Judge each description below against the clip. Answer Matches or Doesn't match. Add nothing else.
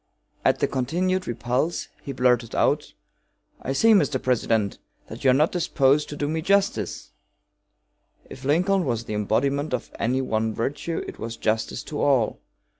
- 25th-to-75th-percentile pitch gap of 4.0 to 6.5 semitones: Matches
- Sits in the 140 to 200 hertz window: Doesn't match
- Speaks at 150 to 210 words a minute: Matches